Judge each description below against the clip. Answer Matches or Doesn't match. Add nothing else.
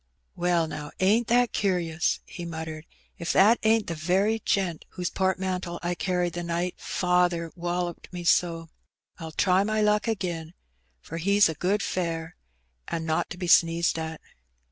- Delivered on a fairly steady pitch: Matches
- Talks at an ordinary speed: Matches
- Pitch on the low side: Doesn't match